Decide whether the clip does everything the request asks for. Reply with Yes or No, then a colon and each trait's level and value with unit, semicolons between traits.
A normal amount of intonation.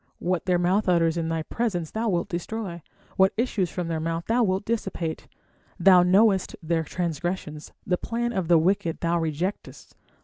Yes: average, 3.1 semitones